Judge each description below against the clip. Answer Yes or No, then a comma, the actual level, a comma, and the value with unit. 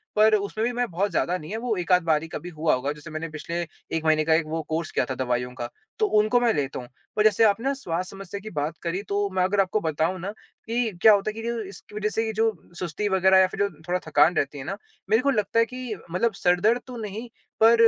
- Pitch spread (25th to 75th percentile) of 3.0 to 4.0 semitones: No, average, 5.2 semitones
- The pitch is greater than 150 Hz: Yes, high, 190 Hz